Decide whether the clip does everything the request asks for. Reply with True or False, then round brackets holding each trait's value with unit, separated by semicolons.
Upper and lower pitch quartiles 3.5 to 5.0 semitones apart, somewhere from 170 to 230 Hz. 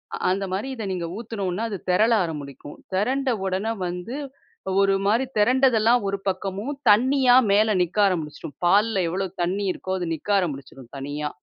True (4.1 semitones; 195 Hz)